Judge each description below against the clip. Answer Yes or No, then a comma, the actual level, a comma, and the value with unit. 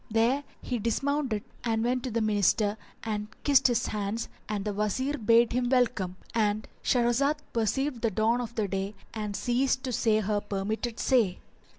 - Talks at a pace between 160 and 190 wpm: Yes, average, 165 wpm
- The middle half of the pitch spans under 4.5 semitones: Yes, average, 2.8 semitones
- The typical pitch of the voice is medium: No, high, 225 Hz